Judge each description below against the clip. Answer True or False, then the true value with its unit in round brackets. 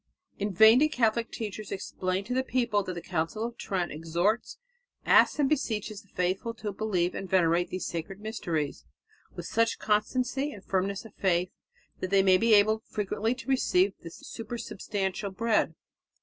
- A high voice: True (205 Hz)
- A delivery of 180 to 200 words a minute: False (165 wpm)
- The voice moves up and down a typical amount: True (3.6 semitones)